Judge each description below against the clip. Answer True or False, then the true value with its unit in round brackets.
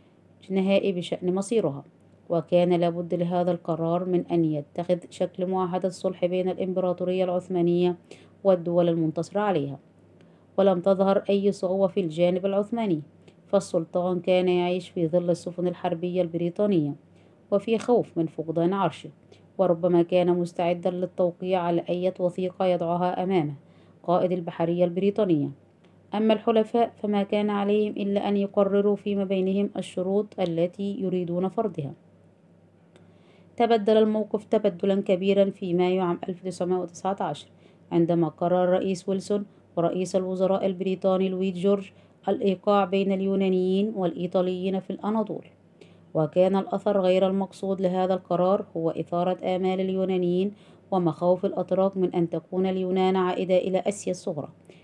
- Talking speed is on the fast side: False (120 wpm)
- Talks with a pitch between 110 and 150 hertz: False (185 Hz)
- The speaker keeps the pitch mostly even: True (1.8 semitones)